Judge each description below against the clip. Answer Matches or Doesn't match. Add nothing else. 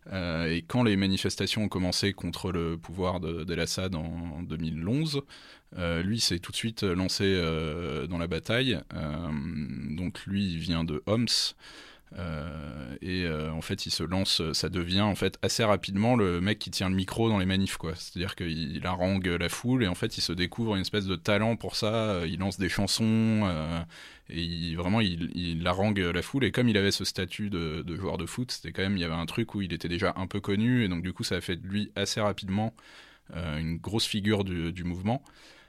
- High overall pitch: Doesn't match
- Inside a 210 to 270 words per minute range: Matches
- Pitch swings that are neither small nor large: Matches